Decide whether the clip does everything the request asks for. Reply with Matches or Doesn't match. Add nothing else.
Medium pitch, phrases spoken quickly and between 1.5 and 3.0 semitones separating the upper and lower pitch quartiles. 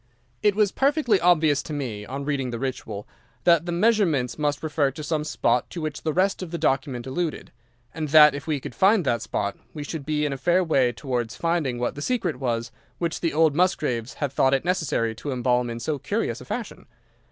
Doesn't match